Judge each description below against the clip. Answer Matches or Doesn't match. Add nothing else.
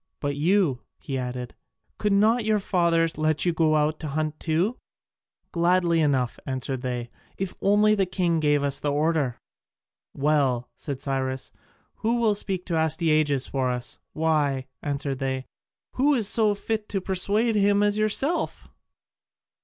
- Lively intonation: Matches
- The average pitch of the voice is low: Doesn't match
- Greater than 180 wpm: Doesn't match